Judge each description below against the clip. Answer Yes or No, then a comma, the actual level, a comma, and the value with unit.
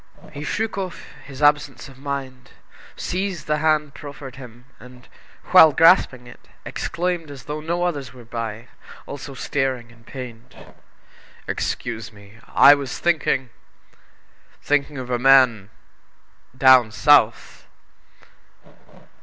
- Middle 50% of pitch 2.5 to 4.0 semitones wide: Yes, average, 3.3 semitones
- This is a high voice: No, low, 135 Hz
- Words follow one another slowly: Yes, slow, 120 wpm